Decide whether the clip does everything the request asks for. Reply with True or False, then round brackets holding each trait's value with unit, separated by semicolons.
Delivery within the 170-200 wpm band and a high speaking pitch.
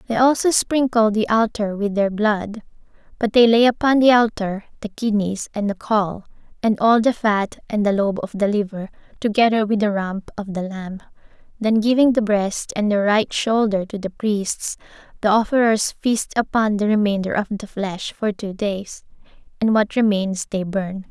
True (180 wpm; 210 Hz)